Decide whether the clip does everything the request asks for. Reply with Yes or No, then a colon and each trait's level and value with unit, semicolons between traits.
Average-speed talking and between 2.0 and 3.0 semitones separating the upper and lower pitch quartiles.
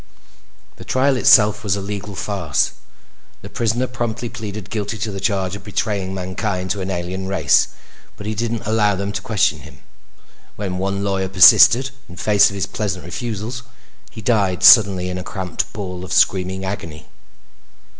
Yes: average, 165 wpm; narrow, 2.6 semitones